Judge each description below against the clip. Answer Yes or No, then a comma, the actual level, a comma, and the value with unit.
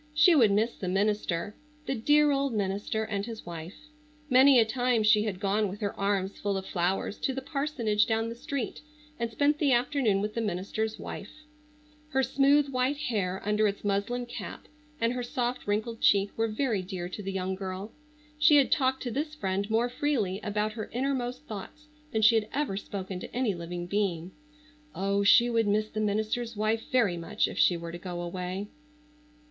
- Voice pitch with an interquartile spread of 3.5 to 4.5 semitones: Yes, average, 4.1 semitones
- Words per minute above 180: Yes, average, 190 wpm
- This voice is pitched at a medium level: No, high, 215 Hz